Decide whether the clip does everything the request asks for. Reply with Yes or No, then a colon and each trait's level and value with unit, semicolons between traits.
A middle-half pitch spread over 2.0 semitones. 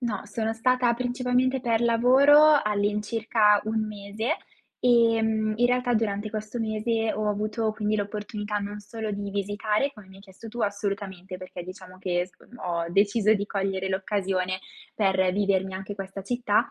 Yes: narrow, 2.5 semitones